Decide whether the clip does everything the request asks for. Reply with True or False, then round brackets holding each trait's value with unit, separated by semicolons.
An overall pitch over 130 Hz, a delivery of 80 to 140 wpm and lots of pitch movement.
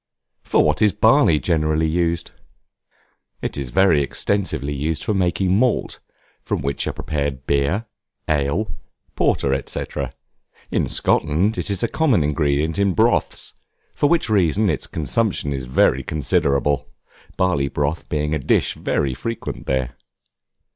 False (80 Hz; 135 wpm; 5.9 semitones)